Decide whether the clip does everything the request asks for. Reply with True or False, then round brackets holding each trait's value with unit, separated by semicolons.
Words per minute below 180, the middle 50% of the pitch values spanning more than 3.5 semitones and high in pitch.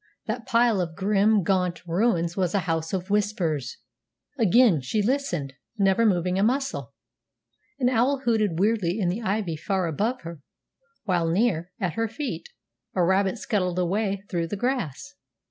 True (155 wpm; 4.5 semitones; 195 Hz)